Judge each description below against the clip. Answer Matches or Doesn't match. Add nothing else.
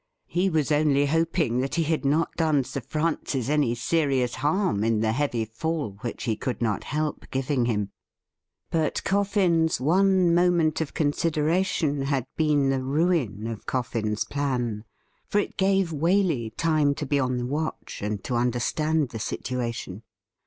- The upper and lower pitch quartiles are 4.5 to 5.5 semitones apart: Matches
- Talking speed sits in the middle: Matches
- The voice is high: Doesn't match